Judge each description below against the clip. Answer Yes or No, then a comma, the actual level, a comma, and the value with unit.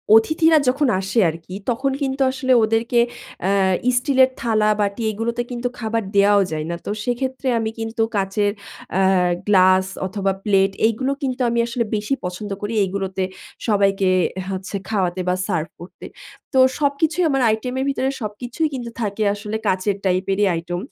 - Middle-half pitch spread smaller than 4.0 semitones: No, average, 4.3 semitones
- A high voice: Yes, high, 210 Hz